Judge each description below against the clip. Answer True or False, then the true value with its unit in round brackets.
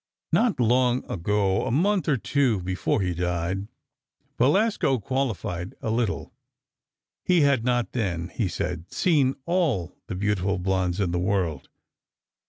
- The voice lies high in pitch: False (105 Hz)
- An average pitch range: False (6.6 semitones)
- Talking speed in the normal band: False (120 wpm)